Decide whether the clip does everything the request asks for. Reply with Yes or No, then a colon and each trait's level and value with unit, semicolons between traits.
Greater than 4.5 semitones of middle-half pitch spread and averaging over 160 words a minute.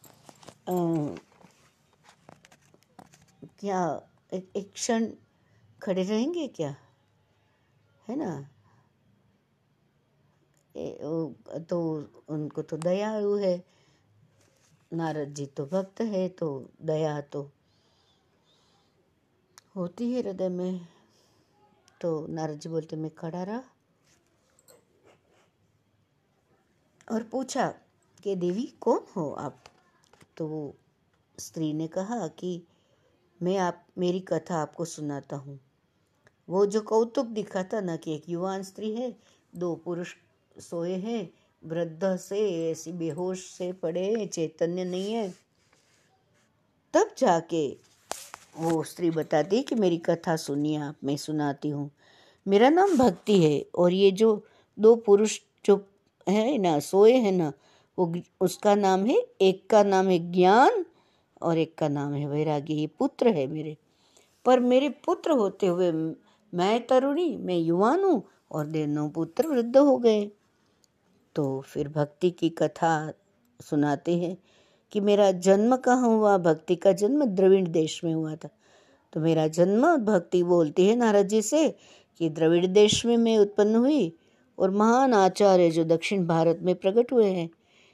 No: average, 4.9 semitones; average, 130 wpm